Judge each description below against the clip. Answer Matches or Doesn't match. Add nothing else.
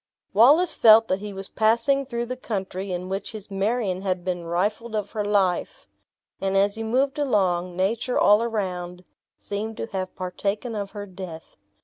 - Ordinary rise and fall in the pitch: Matches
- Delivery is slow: Doesn't match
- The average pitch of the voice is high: Matches